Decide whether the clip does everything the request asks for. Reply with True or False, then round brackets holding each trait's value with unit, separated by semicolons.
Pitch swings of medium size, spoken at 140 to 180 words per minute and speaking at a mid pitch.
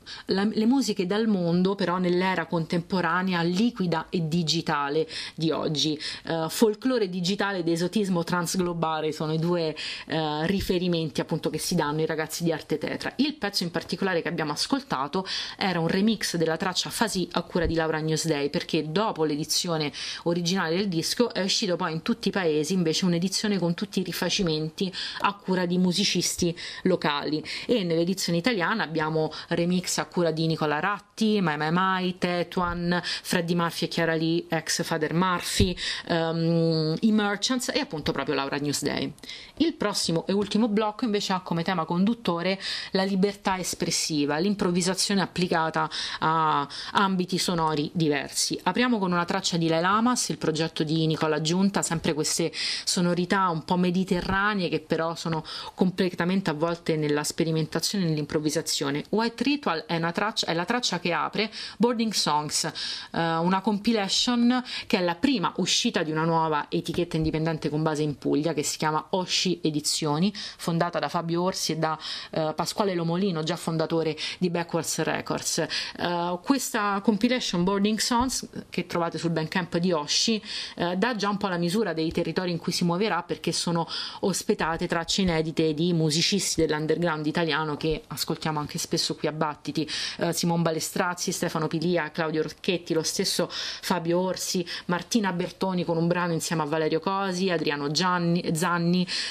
True (3.2 semitones; 160 wpm; 175 Hz)